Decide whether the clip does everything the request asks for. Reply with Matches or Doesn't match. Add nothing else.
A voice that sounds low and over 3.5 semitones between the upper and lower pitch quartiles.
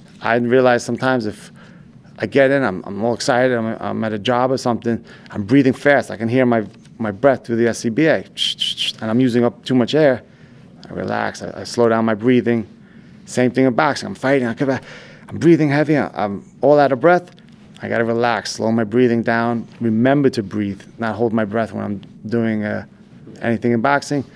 Doesn't match